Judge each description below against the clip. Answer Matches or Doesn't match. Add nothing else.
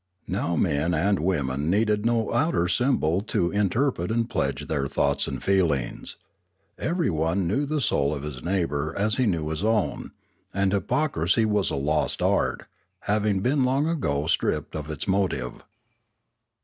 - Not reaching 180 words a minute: Matches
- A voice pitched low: Matches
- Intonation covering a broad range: Matches